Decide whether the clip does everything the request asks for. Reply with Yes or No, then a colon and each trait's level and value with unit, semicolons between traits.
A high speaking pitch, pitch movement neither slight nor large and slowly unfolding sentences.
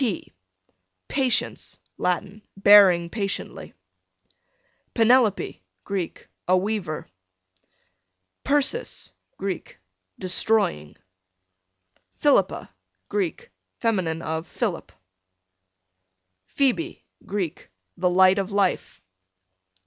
Yes: high, 200 Hz; average, 4.6 semitones; slow, 70 wpm